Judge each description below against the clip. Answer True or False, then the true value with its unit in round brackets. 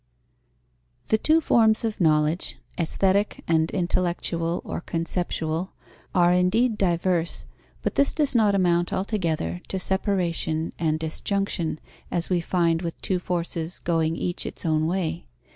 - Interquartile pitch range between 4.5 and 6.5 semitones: False (2.7 semitones)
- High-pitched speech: False (175 Hz)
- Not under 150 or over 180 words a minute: False (135 wpm)